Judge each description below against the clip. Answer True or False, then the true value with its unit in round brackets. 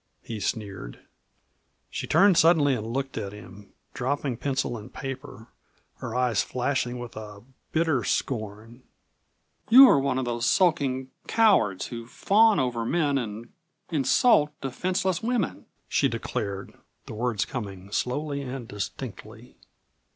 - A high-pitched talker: False (125 Hz)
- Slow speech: True (130 wpm)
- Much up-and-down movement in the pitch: False (4.8 semitones)